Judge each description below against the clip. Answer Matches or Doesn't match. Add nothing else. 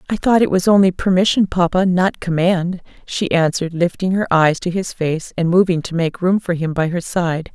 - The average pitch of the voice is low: Doesn't match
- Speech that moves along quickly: Matches